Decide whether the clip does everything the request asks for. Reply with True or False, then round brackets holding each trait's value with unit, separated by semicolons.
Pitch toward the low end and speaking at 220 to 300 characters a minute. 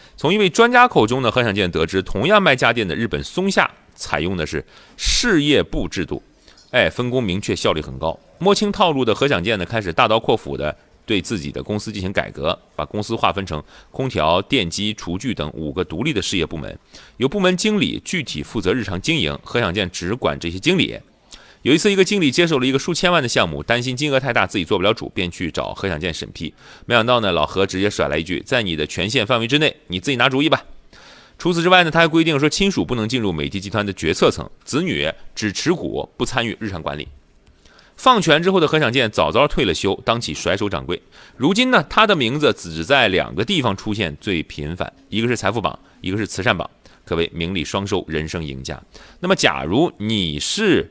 False (105 Hz; 330 characters per minute)